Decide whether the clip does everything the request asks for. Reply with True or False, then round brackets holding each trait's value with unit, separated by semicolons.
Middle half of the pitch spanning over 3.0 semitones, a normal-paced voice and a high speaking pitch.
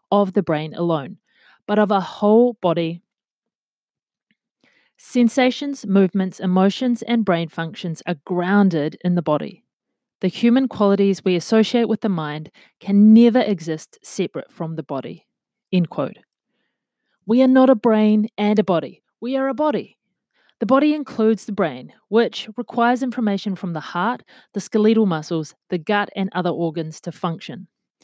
True (5.0 semitones; 150 wpm; 200 Hz)